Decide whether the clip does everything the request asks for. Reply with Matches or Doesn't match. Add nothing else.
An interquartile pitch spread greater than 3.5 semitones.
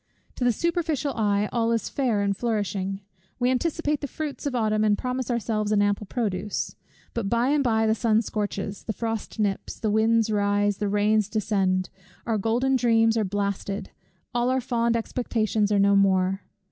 Doesn't match